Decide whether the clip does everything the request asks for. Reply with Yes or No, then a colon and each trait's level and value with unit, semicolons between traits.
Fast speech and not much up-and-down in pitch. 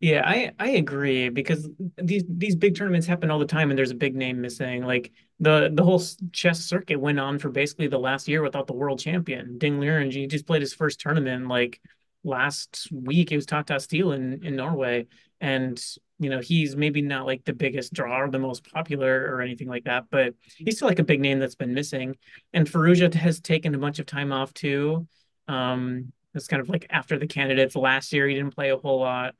No: fast, 220 wpm; average, 3.3 semitones